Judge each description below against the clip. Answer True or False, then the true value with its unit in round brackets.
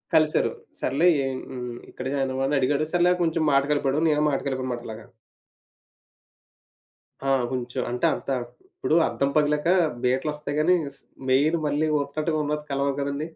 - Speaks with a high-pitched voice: False (145 Hz)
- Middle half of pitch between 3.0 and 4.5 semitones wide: False (2.6 semitones)